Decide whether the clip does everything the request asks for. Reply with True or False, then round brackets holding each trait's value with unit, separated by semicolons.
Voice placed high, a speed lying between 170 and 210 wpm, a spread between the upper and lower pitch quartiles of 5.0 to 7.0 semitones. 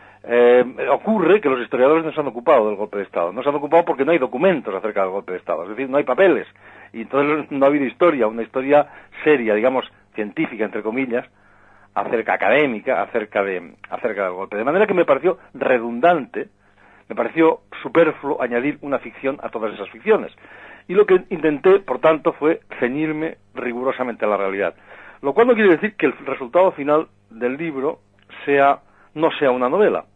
False (135 Hz; 190 wpm; 5.6 semitones)